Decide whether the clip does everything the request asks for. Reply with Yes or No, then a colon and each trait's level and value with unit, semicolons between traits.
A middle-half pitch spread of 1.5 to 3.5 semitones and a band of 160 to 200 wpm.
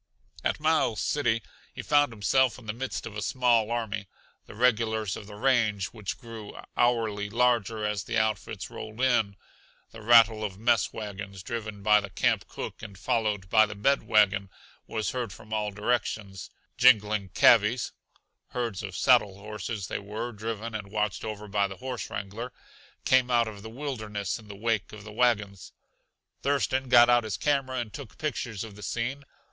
Yes: average, 2.8 semitones; average, 175 wpm